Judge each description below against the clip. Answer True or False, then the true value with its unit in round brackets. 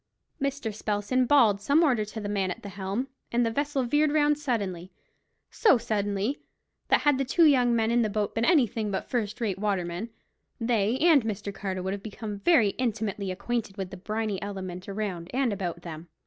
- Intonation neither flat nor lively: True (4.1 semitones)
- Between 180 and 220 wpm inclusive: True (190 wpm)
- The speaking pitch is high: True (215 Hz)